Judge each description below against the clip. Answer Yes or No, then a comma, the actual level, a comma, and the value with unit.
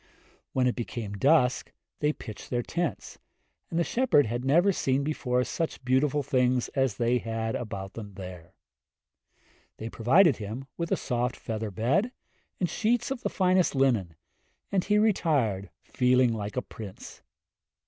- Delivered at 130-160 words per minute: Yes, average, 150 wpm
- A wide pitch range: Yes, wide, 6.1 semitones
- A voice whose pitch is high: No, low, 125 Hz